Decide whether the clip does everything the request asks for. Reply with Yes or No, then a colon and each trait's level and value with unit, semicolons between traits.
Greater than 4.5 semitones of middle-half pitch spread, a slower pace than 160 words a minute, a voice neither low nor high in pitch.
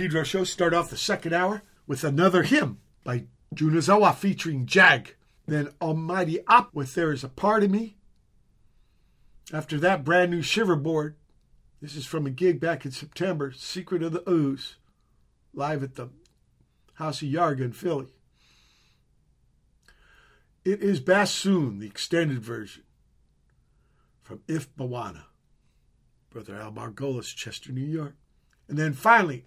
Yes: wide, 5.6 semitones; average, 140 wpm; medium, 150 Hz